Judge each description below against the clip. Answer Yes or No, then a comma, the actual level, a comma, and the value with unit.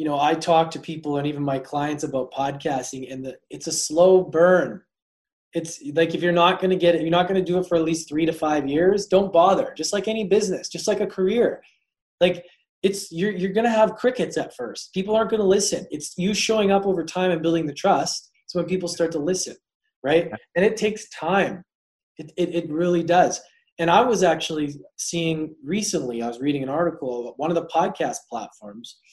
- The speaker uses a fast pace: Yes, fast, 225 wpm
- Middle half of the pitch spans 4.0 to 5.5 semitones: No, average, 3.2 semitones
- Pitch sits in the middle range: Yes, medium, 170 Hz